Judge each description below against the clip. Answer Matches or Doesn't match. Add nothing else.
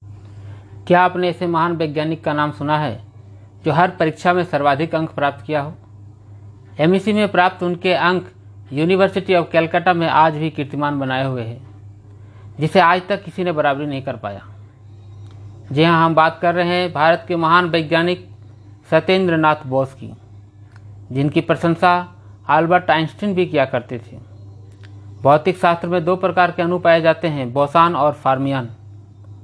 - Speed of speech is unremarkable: Matches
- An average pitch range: Doesn't match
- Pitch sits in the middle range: Matches